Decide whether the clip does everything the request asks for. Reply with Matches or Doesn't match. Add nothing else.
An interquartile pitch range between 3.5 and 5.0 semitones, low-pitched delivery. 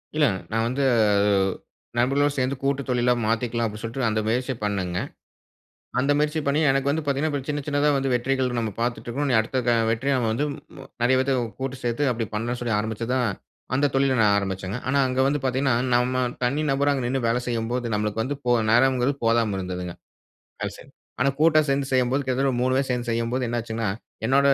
Doesn't match